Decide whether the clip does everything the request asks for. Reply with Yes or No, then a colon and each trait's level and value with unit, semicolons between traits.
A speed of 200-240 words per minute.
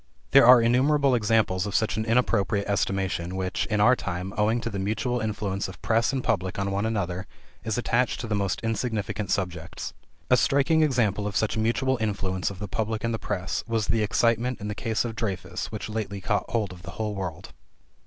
Yes: fast, 205 wpm